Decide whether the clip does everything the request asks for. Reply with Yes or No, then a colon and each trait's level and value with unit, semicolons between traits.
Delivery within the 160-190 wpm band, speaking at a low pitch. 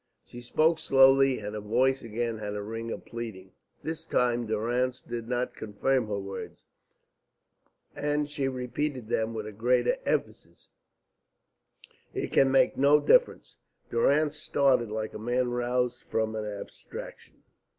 No: average, 140 wpm; low, 120 Hz